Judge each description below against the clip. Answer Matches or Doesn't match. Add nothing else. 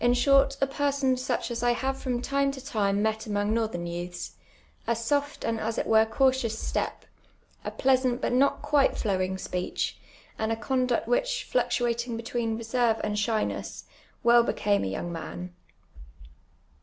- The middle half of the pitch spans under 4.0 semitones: Matches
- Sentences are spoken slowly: Doesn't match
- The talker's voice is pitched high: Matches